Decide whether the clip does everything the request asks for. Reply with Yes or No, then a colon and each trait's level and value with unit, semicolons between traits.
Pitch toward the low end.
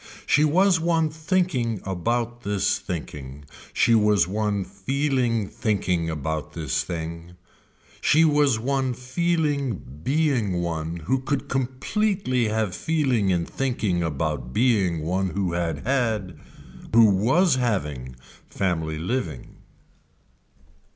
Yes: low, 110 Hz